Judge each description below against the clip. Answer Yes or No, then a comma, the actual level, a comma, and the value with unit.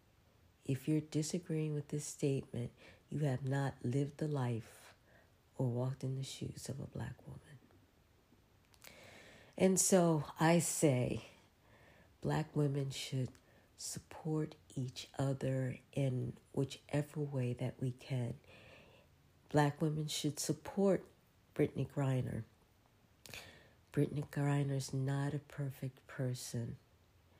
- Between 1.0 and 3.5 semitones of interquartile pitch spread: Yes, average, 3.2 semitones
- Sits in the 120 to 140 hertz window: Yes, low, 135 Hz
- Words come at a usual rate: No, slow, 110 wpm